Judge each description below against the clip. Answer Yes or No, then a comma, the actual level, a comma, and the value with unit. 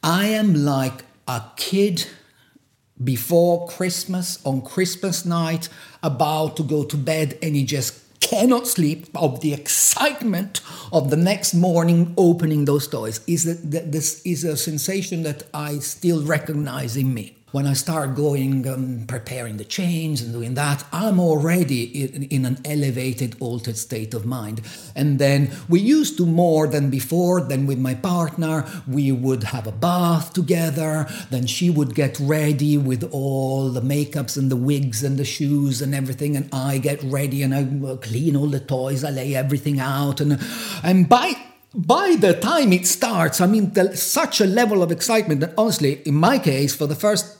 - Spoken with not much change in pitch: No, average, 4.3 semitones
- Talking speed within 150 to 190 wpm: Yes, average, 170 wpm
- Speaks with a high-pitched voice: No, medium, 150 Hz